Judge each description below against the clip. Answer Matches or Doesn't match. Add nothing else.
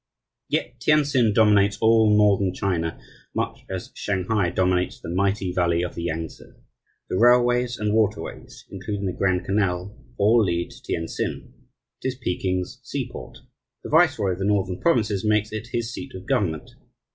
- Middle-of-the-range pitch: Doesn't match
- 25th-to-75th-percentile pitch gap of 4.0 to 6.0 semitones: Doesn't match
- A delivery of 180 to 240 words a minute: Doesn't match